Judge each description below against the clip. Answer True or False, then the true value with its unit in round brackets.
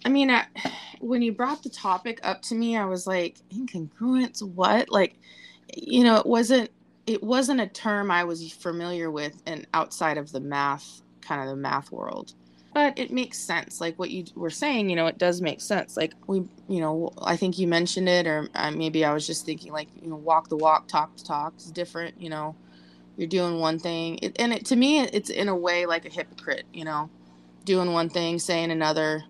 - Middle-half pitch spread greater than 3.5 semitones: True (5.6 semitones)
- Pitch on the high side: False (175 Hz)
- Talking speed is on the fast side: True (215 wpm)